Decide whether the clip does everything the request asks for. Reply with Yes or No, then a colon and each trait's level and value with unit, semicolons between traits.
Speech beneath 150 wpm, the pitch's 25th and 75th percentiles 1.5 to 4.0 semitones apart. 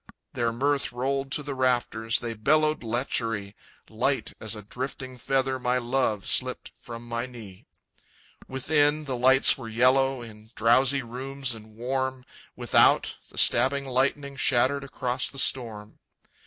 Yes: average, 140 wpm; narrow, 2.6 semitones